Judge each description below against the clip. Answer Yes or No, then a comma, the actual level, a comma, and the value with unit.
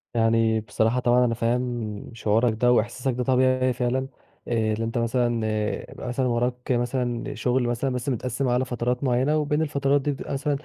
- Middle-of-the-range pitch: No, low, 125 Hz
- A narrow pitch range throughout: Yes, narrow, 1.8 semitones